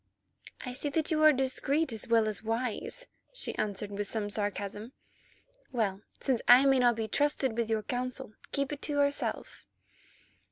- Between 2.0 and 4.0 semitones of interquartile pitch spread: No, average, 4.5 semitones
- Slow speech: No, average, 165 wpm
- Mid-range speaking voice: No, high, 245 Hz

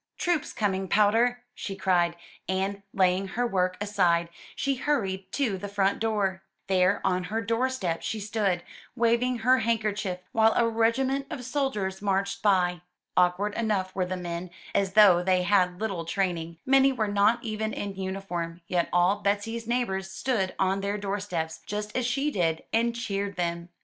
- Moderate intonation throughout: Yes, average, 3.5 semitones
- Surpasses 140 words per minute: Yes, average, 165 wpm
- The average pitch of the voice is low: No, high, 200 Hz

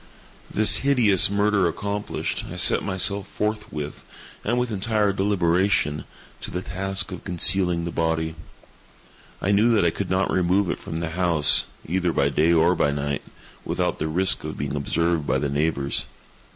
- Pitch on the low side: Yes, very low, 90 Hz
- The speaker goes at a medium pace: Yes, average, 165 wpm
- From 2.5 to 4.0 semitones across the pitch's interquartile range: Yes, average, 3.7 semitones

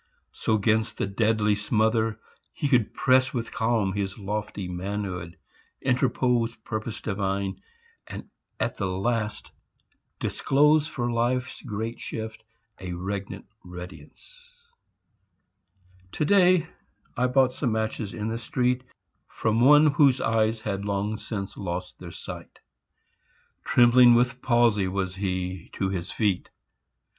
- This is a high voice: No, low, 110 Hz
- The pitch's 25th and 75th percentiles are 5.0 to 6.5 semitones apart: No, average, 3.9 semitones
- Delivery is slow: Yes, slow, 120 wpm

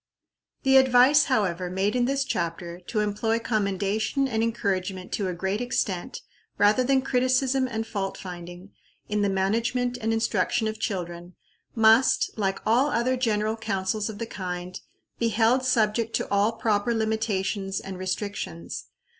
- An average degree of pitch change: Yes, average, 3.7 semitones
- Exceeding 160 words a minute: No, average, 145 wpm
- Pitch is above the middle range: Yes, high, 215 Hz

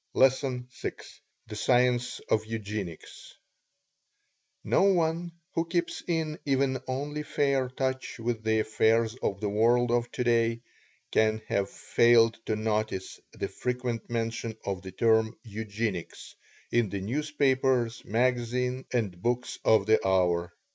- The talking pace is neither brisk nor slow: No, slow, 125 wpm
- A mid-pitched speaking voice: No, low, 115 Hz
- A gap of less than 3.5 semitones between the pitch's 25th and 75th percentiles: Yes, average, 3.0 semitones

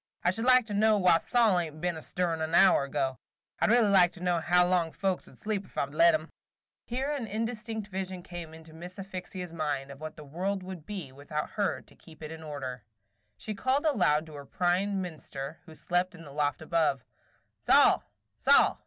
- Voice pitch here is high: No, medium, 175 Hz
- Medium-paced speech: No, fast, 210 wpm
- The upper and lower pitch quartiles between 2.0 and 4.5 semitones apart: Yes, average, 4.1 semitones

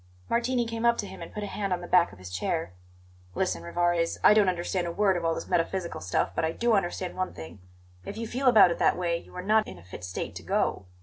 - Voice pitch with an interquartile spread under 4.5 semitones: Yes, average, 4.1 semitones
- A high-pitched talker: No, medium, 180 Hz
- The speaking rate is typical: No, fast, 265 wpm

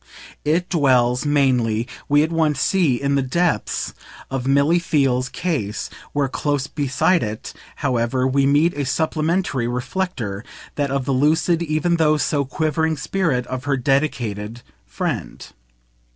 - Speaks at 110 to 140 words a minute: Yes, slow, 135 wpm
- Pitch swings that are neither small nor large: Yes, average, 3.8 semitones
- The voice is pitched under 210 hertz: Yes, medium, 140 Hz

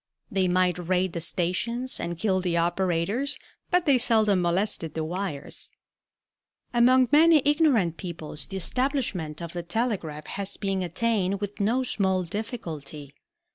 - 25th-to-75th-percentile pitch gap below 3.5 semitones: No, wide, 5.4 semitones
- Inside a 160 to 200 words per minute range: No, slow, 135 wpm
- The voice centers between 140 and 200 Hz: Yes, high, 190 Hz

